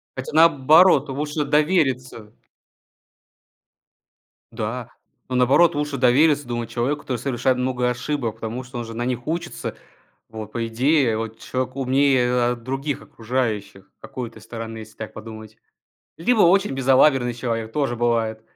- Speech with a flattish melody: No, average, 3.6 semitones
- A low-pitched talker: Yes, low, 125 Hz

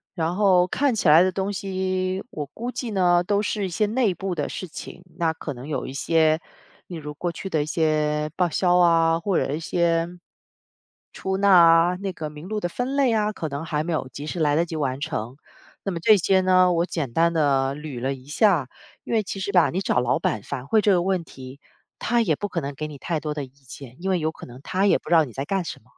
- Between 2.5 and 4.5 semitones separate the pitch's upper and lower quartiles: Yes, average, 4.2 semitones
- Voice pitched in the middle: Yes, medium, 170 Hz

